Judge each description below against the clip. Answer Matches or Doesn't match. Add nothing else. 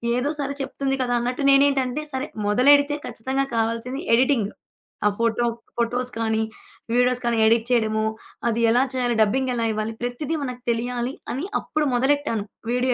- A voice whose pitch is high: Matches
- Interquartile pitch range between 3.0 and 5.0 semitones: Doesn't match